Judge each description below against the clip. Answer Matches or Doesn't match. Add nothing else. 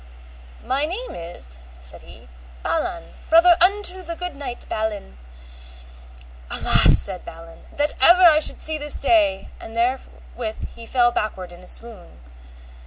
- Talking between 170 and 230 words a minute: Doesn't match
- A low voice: Doesn't match